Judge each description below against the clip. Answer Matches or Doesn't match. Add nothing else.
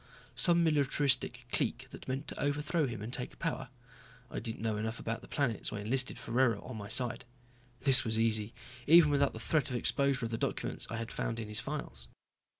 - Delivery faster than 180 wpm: Matches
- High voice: Doesn't match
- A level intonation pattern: Doesn't match